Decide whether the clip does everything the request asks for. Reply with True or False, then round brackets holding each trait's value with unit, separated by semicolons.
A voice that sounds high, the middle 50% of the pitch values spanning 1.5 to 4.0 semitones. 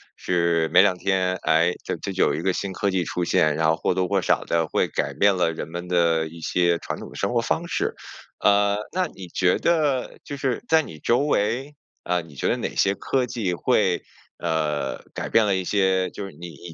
False (90 Hz; 3.5 semitones)